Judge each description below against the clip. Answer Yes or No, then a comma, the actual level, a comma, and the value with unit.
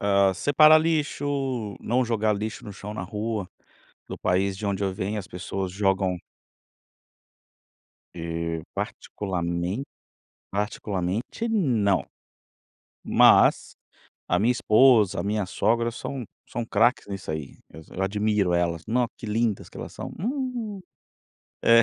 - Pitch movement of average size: Yes, average, 3.9 semitones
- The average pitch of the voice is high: No, low, 105 Hz